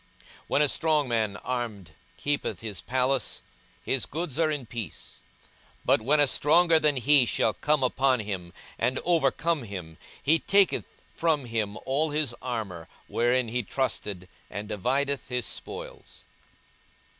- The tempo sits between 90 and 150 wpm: Yes, average, 145 wpm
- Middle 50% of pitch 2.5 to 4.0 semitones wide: No, average, 5.2 semitones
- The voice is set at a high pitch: No, low, 130 Hz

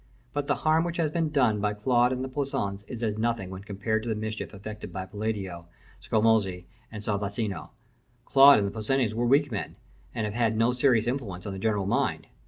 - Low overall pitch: Yes, low, 110 Hz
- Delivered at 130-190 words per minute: No, fast, 205 wpm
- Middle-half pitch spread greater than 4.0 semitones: No, average, 3.7 semitones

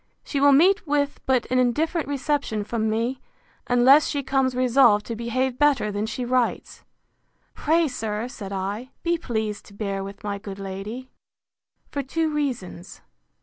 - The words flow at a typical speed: Yes, average, 155 wpm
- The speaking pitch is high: Yes, very high, 250 Hz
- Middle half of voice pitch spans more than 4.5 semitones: Yes, average, 5.0 semitones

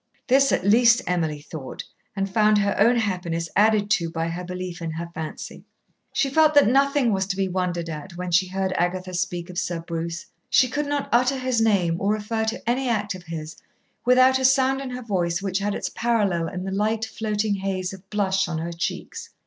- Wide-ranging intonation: No, average, 4.8 semitones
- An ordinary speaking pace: No, fast, 210 wpm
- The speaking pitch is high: Yes, high, 195 Hz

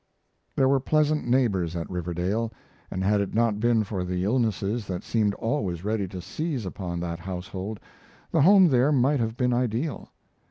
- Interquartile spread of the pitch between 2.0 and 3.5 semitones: No, average, 5.3 semitones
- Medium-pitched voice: No, low, 110 Hz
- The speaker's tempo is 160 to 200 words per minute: Yes, average, 170 wpm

